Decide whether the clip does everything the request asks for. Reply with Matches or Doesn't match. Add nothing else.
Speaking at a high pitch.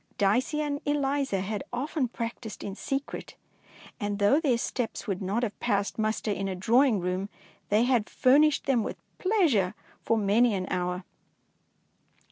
Matches